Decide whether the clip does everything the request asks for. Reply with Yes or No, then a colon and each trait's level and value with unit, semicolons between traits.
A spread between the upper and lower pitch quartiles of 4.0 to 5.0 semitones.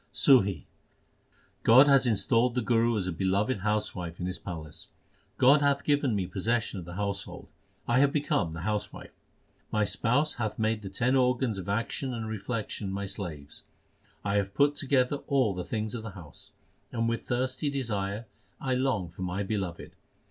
Yes: average, 4.6 semitones